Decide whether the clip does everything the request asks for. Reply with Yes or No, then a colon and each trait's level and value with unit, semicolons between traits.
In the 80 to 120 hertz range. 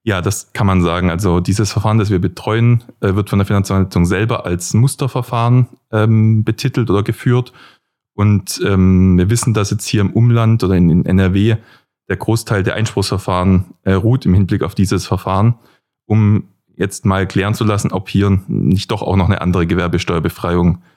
Yes: low, 100 Hz